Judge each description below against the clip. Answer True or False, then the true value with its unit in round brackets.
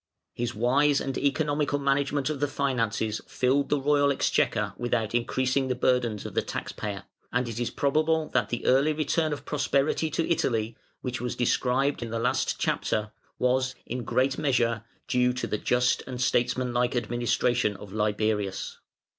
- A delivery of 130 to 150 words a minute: False (165 wpm)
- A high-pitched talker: False (125 Hz)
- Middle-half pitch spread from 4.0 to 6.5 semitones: False (3.0 semitones)